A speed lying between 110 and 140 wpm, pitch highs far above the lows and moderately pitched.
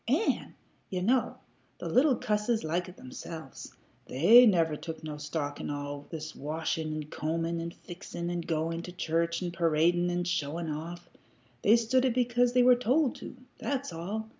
No: average, 170 wpm; wide, 5.8 semitones; medium, 170 Hz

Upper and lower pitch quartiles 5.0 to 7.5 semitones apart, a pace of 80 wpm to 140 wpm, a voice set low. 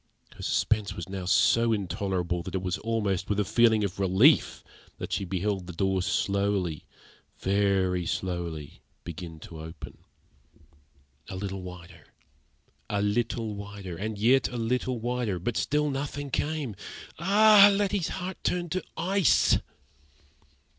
Yes: average, 5.3 semitones; slow, 135 wpm; low, 100 Hz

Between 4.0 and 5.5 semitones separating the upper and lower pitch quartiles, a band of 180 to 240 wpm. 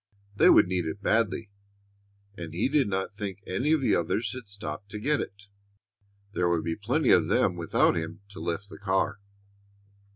Yes: average, 4.3 semitones; average, 185 wpm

